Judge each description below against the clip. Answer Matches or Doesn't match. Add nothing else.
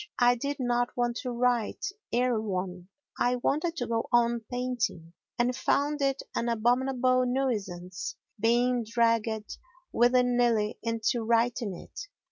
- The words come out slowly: Matches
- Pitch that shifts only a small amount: Matches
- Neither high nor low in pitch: Doesn't match